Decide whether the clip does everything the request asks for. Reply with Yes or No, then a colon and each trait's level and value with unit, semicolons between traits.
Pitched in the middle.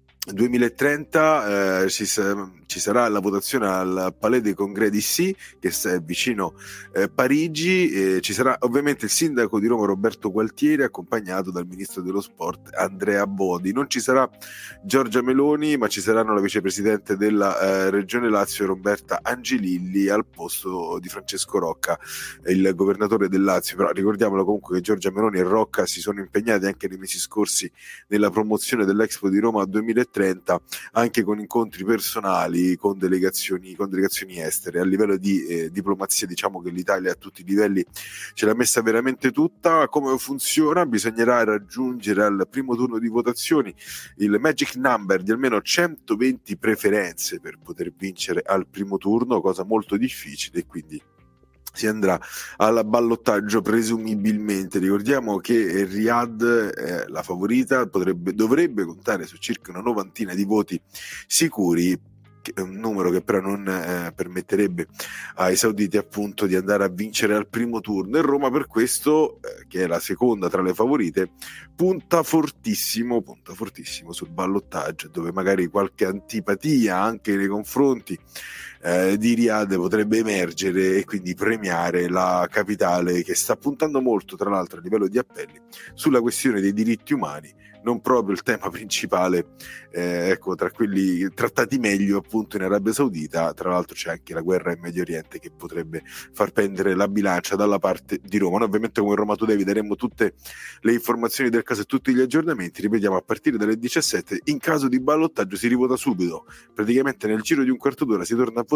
No: low, 105 Hz